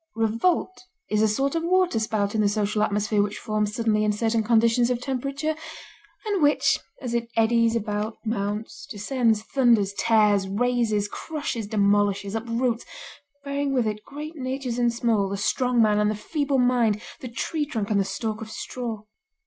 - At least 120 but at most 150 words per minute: No, average, 165 wpm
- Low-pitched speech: No, high, 225 Hz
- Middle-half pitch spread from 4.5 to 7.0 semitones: No, average, 3.2 semitones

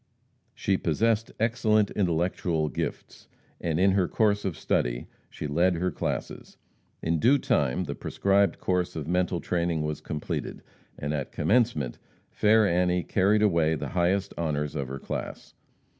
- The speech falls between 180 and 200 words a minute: No, average, 145 wpm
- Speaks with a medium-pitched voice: No, very low, 90 Hz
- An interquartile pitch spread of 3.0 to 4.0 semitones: No, average, 4.5 semitones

